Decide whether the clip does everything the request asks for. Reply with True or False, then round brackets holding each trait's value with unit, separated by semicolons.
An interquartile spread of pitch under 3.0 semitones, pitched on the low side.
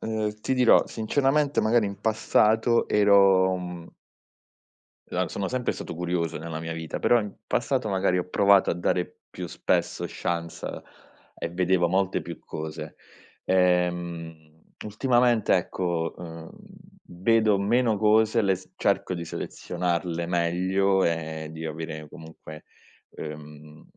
False (4.3 semitones; 90 Hz)